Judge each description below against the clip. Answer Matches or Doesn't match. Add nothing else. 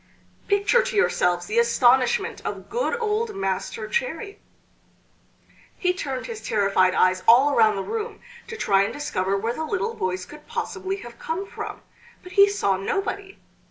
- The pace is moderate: Matches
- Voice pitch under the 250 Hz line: Doesn't match